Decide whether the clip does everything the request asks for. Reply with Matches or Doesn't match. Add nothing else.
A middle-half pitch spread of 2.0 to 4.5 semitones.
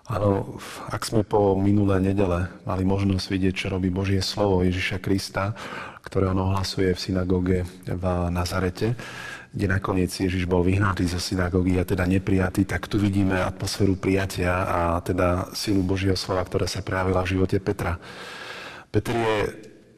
Doesn't match